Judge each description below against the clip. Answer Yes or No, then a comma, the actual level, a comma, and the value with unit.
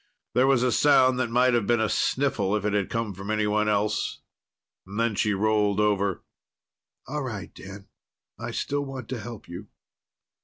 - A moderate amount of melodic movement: Yes, average, 3.6 semitones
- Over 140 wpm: Yes, average, 170 wpm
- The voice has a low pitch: Yes, low, 110 Hz